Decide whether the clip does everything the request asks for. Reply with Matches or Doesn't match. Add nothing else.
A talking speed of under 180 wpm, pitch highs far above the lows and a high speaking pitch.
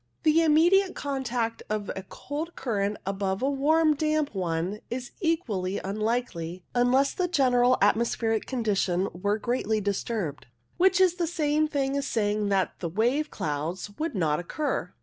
Matches